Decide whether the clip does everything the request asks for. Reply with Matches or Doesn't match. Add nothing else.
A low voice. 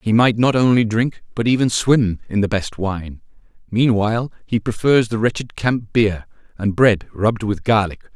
Matches